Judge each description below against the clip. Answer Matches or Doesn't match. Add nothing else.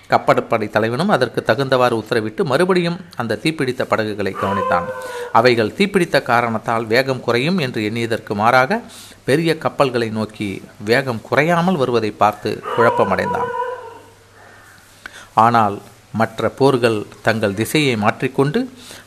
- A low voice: Matches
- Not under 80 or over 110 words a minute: Matches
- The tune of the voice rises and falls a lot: Matches